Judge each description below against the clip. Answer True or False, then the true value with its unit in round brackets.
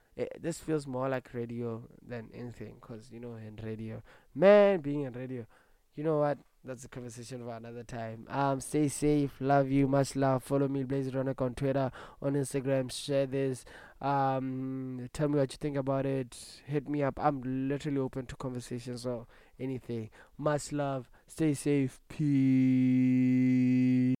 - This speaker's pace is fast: False (165 wpm)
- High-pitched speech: False (130 Hz)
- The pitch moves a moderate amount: False (2.1 semitones)